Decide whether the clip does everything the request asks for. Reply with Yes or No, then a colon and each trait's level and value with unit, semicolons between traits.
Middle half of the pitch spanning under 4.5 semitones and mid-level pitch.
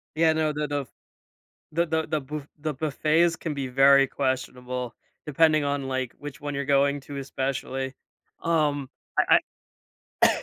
Yes: narrow, 2.4 semitones; medium, 145 Hz